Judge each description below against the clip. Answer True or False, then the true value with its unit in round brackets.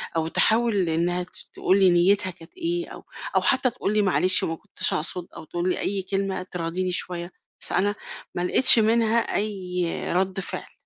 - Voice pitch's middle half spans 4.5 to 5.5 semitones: False (3.2 semitones)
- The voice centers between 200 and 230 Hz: False (190 Hz)